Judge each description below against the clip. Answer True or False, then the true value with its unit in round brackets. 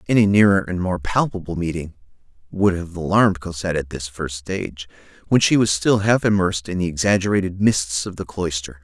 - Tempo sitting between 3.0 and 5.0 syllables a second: False (5.7 syllables/s)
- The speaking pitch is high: False (90 Hz)